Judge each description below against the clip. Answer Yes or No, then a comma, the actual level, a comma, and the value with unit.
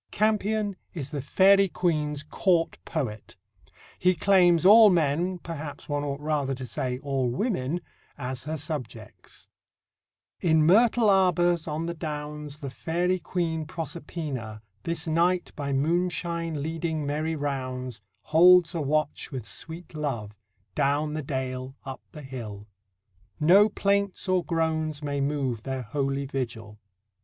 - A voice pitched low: No, medium, 155 Hz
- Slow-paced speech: Yes, slow, 130 wpm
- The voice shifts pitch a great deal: No, average, 4.1 semitones